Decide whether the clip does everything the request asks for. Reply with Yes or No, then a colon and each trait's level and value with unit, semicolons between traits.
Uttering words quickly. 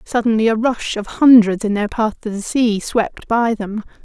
Yes: fast, 210 wpm